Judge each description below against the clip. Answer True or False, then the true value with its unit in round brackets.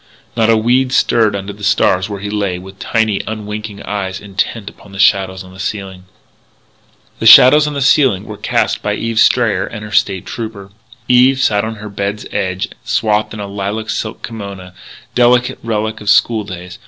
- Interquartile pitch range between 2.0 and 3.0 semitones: True (2.4 semitones)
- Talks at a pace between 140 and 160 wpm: False (185 wpm)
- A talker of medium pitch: False (105 Hz)